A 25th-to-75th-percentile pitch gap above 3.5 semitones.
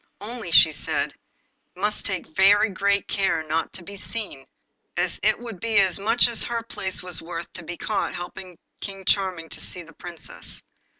No: average, 3.2 semitones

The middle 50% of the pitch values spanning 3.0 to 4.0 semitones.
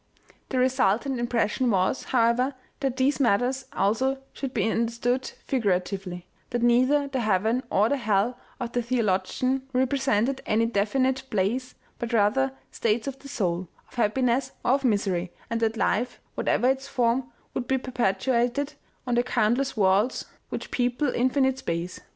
Yes: average, 3.6 semitones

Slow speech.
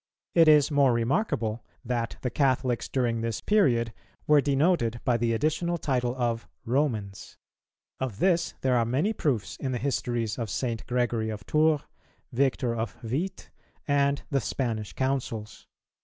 No: average, 145 wpm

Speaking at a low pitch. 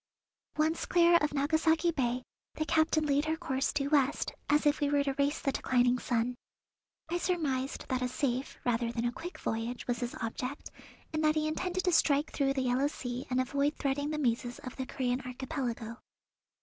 No: very high, 275 Hz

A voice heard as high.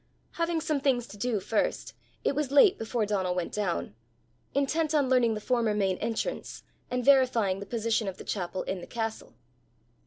Yes: high, 230 Hz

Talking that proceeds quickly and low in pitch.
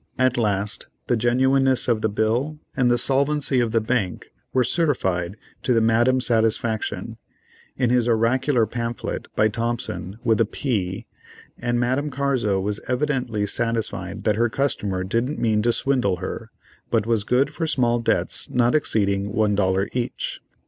No: average, 155 wpm; low, 115 Hz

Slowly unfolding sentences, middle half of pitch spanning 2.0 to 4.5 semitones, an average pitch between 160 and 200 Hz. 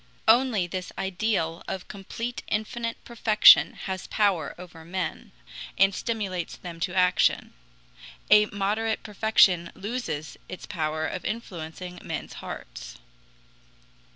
Yes: slow, 110 wpm; average, 3.8 semitones; high, 190 Hz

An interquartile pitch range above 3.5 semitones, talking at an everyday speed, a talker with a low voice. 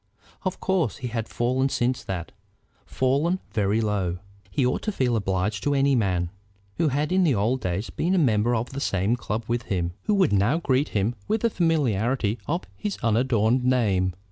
Yes: wide, 5.6 semitones; average, 190 wpm; low, 120 Hz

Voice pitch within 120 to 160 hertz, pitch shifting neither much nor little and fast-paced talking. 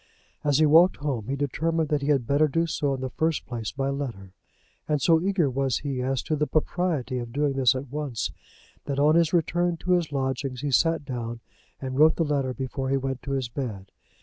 Yes: medium, 140 Hz; average, 3.0 semitones; fast, 220 wpm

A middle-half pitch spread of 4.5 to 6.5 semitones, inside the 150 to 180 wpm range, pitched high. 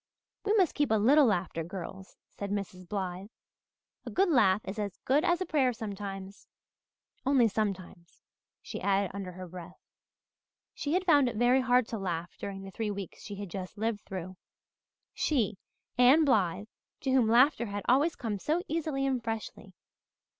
Yes: wide, 5.5 semitones; average, 170 wpm; high, 210 Hz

